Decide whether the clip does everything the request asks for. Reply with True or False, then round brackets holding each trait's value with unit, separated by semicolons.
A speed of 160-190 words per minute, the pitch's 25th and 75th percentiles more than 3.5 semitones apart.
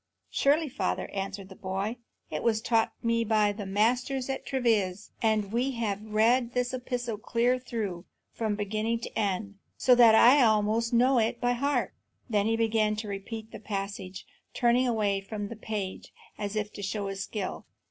False (180 wpm; 2.8 semitones)